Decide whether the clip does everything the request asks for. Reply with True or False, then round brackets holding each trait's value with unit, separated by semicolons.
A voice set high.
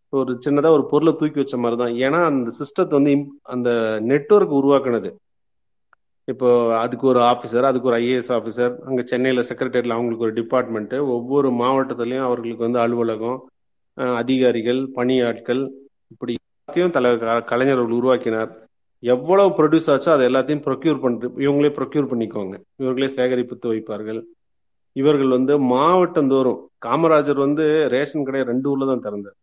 False (125 Hz)